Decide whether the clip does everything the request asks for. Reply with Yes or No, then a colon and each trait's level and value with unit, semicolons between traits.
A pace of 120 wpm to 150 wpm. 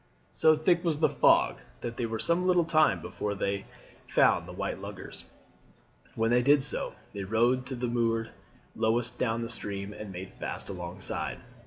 No: average, 175 wpm